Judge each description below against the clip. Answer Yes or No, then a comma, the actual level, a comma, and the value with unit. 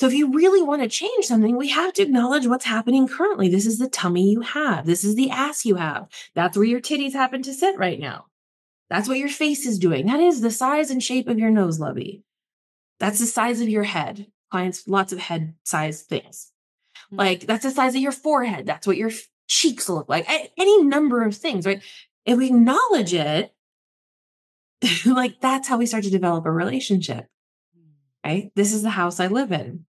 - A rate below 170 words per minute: No, fast, 205 wpm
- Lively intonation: Yes, wide, 6.0 semitones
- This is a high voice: Yes, high, 225 Hz